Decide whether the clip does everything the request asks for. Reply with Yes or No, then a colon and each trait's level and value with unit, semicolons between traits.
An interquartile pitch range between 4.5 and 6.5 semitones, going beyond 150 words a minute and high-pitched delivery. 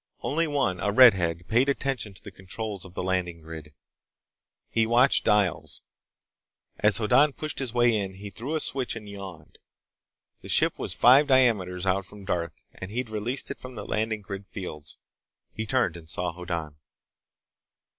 No: average, 5.0 semitones; average, 165 wpm; low, 105 Hz